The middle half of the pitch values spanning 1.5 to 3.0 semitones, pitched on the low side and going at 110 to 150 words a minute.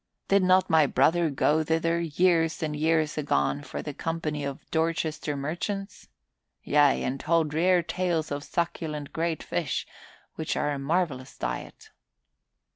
No: narrow, 2.5 semitones; medium, 160 Hz; average, 140 wpm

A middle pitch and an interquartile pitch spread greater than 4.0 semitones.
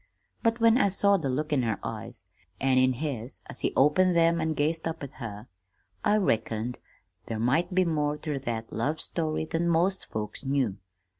Yes: medium, 150 Hz; average, 5.3 semitones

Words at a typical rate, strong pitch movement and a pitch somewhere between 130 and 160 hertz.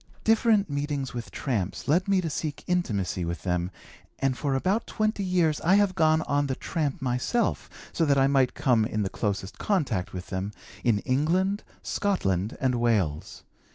Yes: average, 170 wpm; wide, 8.8 semitones; medium, 140 Hz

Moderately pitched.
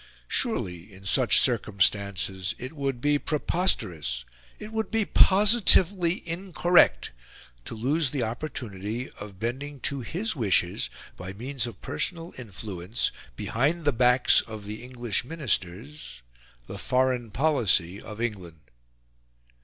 No: low, 125 Hz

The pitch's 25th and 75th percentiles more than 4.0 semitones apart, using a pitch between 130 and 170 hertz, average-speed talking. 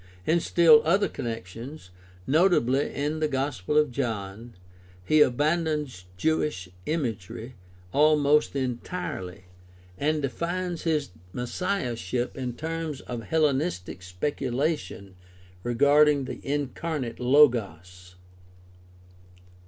No: average, 4.9 semitones; medium, 140 Hz; slow, 90 wpm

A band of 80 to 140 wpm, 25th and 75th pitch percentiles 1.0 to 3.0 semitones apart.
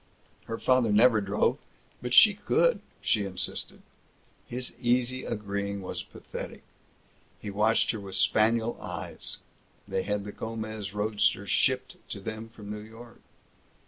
Yes: slow, 135 wpm; narrow, 2.4 semitones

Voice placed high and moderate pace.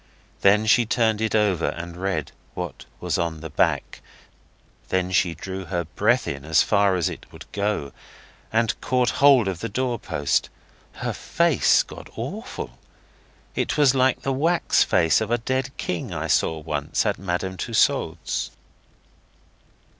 No: very low, 95 Hz; average, 155 wpm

